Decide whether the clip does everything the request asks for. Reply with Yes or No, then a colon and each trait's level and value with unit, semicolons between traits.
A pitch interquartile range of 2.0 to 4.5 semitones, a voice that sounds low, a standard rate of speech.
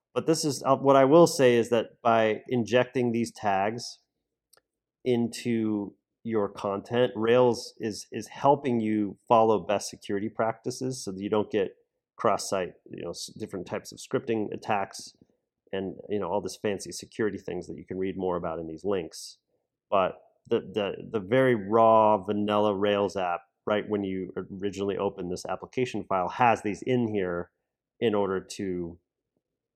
Yes: average, 4.0 semitones; low, 105 Hz; average, 165 wpm